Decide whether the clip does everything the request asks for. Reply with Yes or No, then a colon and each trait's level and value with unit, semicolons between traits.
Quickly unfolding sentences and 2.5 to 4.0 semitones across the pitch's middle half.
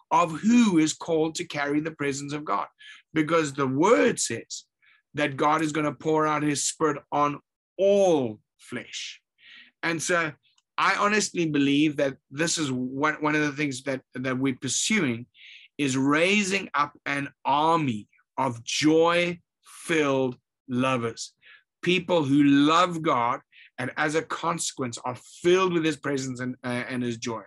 No: average, 150 wpm; average, 3.7 semitones